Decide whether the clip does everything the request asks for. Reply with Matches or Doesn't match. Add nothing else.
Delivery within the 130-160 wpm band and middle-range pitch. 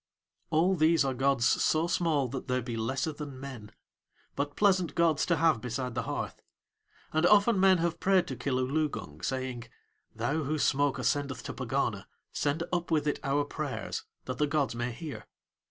Doesn't match